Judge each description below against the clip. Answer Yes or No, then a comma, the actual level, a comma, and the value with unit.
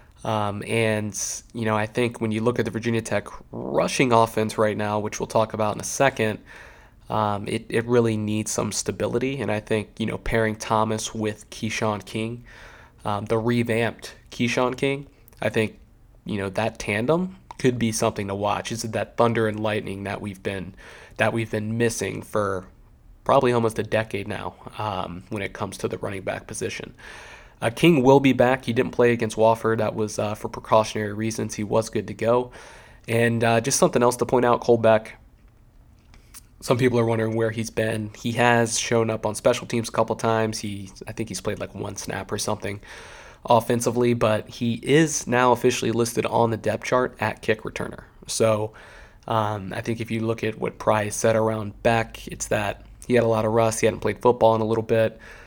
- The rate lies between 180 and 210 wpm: Yes, average, 200 wpm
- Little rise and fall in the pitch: Yes, narrow, 1.7 semitones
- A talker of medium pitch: No, low, 110 Hz